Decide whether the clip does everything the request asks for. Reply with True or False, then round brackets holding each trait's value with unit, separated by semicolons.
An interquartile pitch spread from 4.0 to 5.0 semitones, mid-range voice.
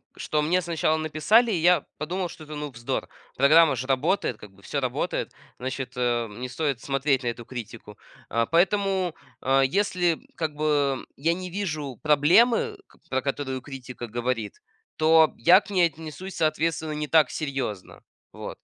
True (4.6 semitones; 150 Hz)